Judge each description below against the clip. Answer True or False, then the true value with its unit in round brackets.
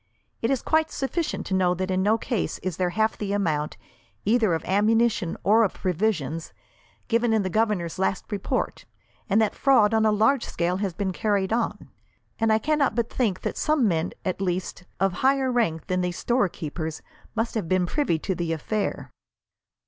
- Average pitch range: True (4.0 semitones)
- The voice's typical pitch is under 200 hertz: False (205 Hz)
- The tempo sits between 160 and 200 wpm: True (185 wpm)